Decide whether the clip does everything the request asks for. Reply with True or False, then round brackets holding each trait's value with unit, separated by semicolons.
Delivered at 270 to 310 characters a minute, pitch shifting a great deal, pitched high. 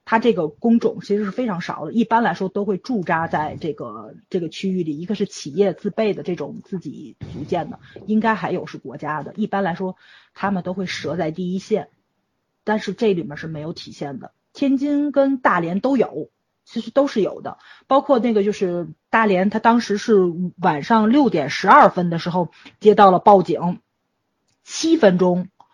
False (275 characters per minute; 4.2 semitones; 200 Hz)